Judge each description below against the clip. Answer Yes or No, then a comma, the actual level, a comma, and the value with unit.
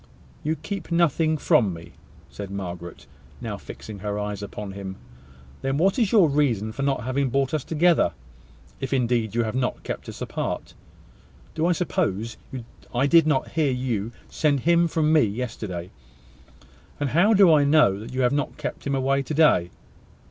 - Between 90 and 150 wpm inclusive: No, average, 175 wpm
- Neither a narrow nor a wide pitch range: No, wide, 6.6 semitones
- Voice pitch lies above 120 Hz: Yes, low, 135 Hz